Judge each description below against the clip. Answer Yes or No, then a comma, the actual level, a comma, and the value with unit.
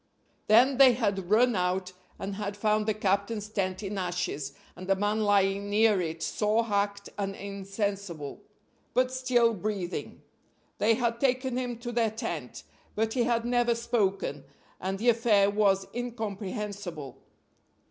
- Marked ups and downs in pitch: No, average, 3.1 semitones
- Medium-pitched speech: No, high, 205 Hz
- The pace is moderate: Yes, average, 145 wpm